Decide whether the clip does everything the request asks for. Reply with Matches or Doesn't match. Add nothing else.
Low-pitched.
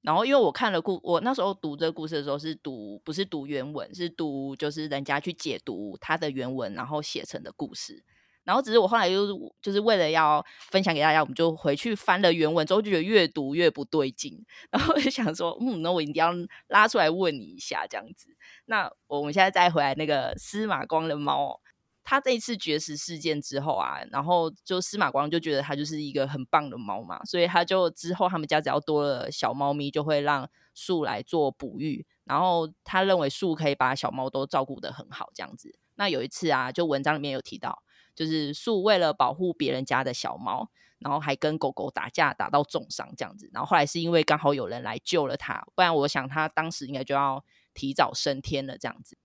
Doesn't match